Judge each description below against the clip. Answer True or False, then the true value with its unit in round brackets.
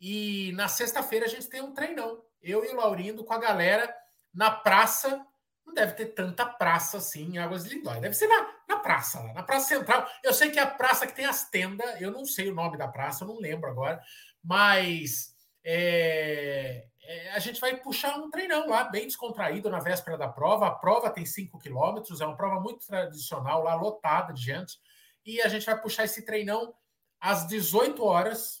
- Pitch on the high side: True (215 Hz)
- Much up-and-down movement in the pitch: True (5.8 semitones)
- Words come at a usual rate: False (205 wpm)